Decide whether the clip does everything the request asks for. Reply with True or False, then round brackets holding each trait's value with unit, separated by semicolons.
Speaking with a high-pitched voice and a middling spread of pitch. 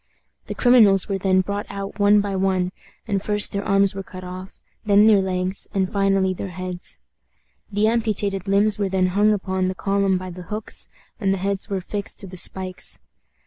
False (195 Hz; 1.5 semitones)